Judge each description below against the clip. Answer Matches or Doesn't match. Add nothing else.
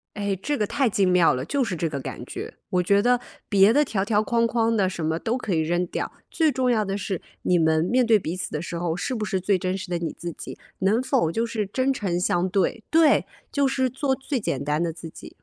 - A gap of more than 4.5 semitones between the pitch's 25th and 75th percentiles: Matches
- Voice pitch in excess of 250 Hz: Doesn't match